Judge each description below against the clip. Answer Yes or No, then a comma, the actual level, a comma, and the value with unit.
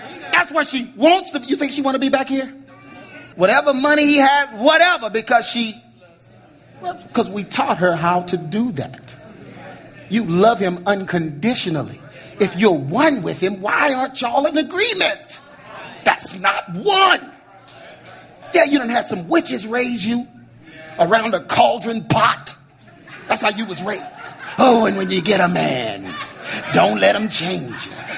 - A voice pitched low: No, high, 235 Hz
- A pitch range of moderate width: No, wide, 7.0 semitones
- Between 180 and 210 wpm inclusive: No, average, 160 wpm